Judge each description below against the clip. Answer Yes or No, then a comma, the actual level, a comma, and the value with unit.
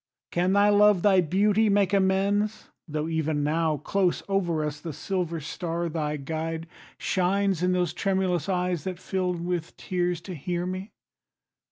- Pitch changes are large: No, average, 2.9 semitones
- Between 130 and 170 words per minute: Yes, average, 155 wpm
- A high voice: No, medium, 180 Hz